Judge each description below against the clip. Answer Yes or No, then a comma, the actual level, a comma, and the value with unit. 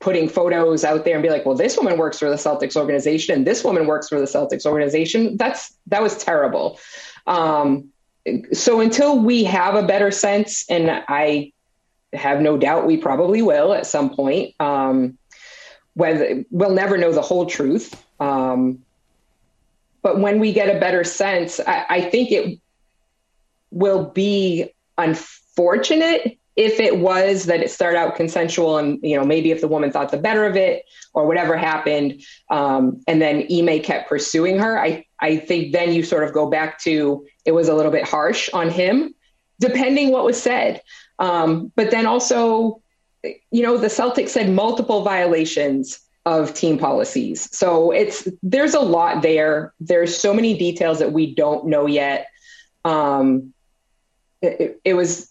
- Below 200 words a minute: Yes, average, 170 wpm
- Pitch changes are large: Yes, wide, 5.7 semitones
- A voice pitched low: No, medium, 170 Hz